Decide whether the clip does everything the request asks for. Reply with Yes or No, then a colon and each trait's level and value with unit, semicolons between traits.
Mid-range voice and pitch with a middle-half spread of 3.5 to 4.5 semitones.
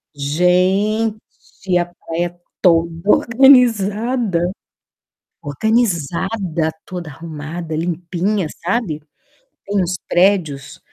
Yes: medium, 180 Hz; average, 3.9 semitones